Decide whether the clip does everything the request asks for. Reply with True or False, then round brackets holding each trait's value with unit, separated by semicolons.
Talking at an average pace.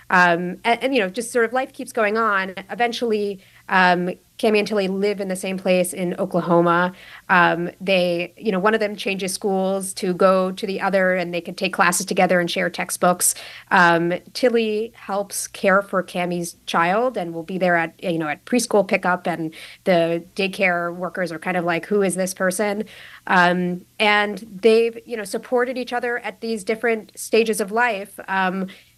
True (190 wpm)